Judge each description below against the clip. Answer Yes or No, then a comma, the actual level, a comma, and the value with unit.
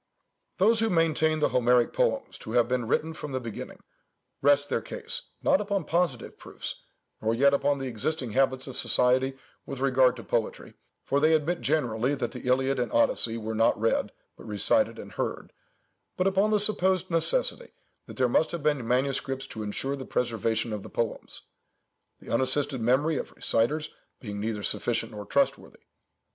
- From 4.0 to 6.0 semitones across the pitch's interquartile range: Yes, average, 5.1 semitones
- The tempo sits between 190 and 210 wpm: No, average, 165 wpm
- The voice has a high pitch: No, low, 135 Hz